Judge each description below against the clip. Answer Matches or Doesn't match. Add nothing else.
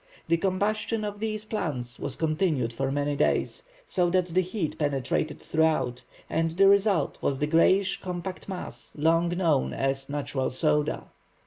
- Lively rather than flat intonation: Doesn't match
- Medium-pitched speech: Matches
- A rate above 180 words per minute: Doesn't match